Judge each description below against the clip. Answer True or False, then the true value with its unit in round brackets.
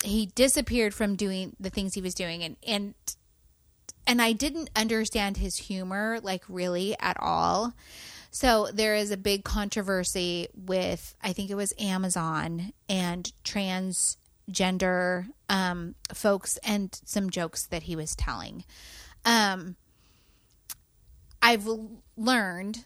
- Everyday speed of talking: False (125 wpm)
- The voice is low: False (200 Hz)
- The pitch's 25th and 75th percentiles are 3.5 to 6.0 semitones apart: False (2.9 semitones)